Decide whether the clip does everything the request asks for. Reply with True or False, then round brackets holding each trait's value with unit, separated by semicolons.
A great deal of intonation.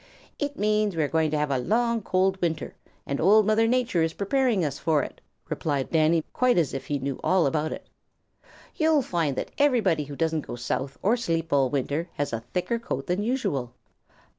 True (7.0 semitones)